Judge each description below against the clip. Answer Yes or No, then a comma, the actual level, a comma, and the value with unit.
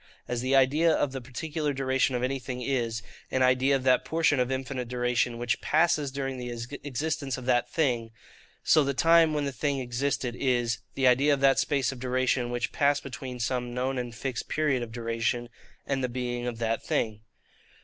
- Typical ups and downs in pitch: No, narrow, 2.2 semitones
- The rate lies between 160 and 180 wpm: No, average, 190 wpm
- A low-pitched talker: Yes, low, 130 Hz